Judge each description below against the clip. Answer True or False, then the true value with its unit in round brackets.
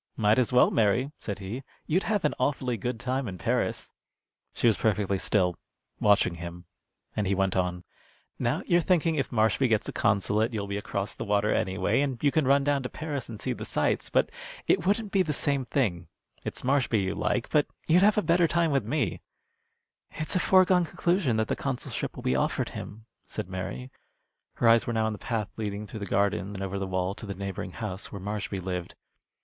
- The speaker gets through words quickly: True (210 wpm)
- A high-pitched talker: False (110 Hz)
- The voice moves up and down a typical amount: False (6.1 semitones)